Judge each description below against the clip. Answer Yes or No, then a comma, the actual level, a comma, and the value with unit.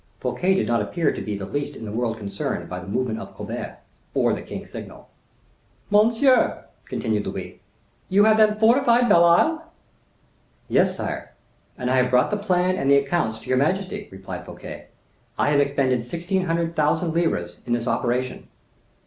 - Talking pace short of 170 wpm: No, average, 175 wpm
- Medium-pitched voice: Yes, medium, 155 Hz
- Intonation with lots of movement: Yes, wide, 7.8 semitones